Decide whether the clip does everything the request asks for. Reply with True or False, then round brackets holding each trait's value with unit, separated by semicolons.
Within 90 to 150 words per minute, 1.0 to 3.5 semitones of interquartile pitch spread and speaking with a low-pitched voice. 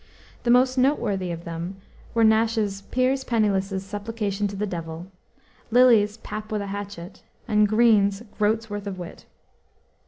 False (145 wpm; 2.6 semitones; 205 Hz)